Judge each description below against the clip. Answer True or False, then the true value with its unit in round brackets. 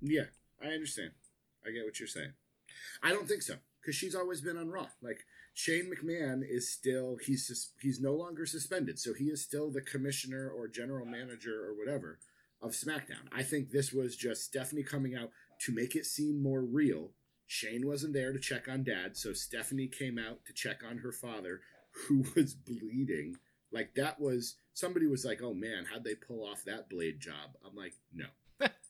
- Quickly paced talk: False (190 wpm)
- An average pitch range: True (3.2 semitones)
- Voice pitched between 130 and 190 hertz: True (135 Hz)